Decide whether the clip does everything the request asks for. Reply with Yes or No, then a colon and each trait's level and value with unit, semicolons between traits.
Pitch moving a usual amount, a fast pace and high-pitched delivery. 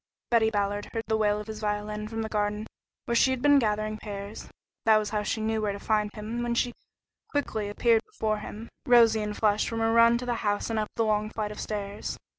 No: narrow, 1.5 semitones; fast, 235 wpm; high, 215 Hz